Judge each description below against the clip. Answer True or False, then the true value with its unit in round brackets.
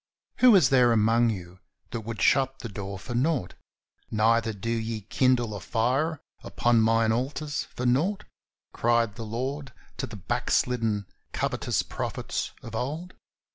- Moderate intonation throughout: True (3.0 semitones)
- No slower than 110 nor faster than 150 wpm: True (145 wpm)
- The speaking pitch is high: False (115 Hz)